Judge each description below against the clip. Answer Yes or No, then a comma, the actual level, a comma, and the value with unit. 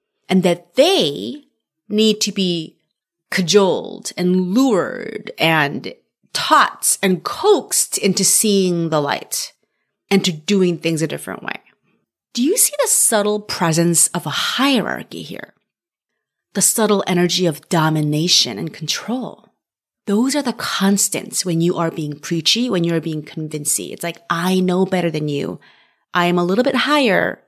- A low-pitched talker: No, medium, 185 Hz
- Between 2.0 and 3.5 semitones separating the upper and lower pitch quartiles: No, average, 4.4 semitones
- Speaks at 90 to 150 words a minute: Yes, average, 145 wpm